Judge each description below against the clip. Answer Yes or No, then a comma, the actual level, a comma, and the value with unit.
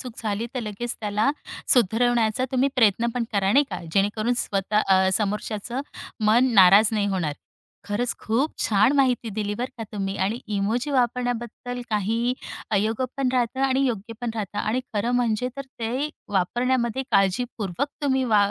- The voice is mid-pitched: No, high, 225 Hz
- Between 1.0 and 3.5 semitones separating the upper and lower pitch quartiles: Yes, average, 3.2 semitones